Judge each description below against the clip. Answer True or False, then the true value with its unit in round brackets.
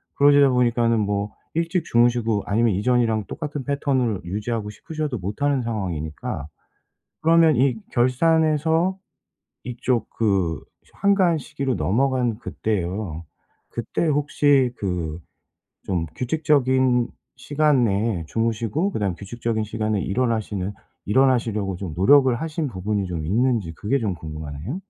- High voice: False (120 Hz)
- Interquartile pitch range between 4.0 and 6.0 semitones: True (5.7 semitones)